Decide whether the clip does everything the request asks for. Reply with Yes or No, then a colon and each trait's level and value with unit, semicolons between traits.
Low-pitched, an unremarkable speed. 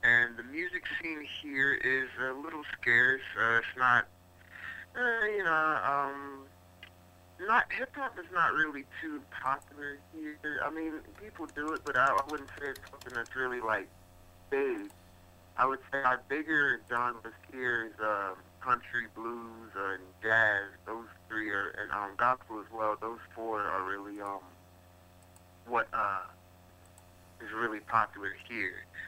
Yes: low, 115 Hz; average, 145 wpm